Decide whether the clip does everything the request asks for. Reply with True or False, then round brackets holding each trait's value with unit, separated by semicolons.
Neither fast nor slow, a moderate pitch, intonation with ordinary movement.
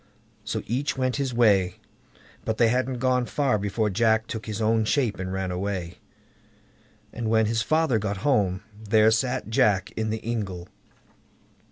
False (160 wpm; 110 Hz; 3.1 semitones)